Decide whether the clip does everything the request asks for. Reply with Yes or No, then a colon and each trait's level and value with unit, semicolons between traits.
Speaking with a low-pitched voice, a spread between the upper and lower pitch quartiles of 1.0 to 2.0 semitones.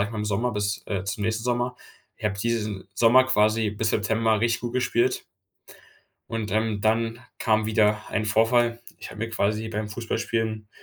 Yes: low, 110 Hz; narrow, 1.6 semitones